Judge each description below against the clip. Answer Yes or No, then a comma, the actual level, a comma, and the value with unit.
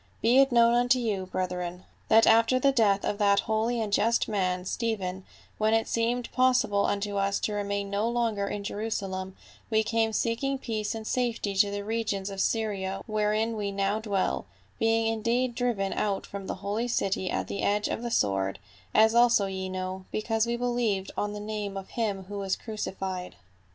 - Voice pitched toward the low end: No, high, 210 Hz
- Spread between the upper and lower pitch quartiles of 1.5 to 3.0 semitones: Yes, average, 2.7 semitones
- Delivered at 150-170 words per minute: No, average, 190 wpm